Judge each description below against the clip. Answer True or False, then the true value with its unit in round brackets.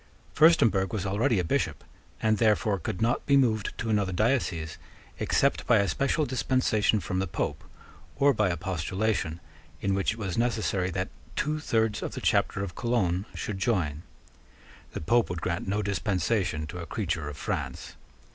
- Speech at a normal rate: True (170 wpm)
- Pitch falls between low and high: False (100 Hz)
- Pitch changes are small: False (4.1 semitones)